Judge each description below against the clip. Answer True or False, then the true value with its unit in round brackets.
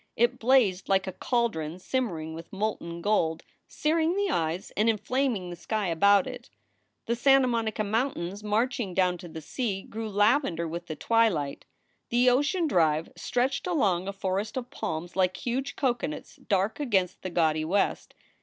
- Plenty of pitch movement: True (5.9 semitones)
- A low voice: False (205 Hz)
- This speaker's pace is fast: False (160 wpm)